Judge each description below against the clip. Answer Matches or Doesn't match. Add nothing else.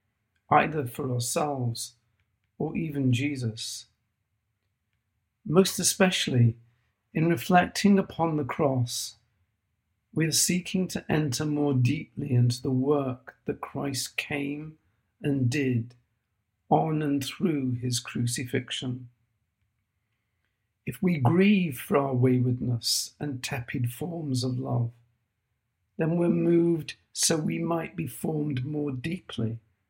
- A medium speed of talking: Doesn't match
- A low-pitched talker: Matches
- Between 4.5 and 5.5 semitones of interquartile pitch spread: Matches